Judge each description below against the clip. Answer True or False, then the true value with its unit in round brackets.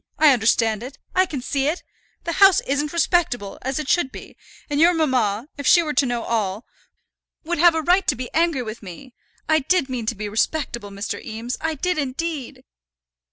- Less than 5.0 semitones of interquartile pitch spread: False (5.5 semitones)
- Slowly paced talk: False (200 wpm)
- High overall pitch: True (275 Hz)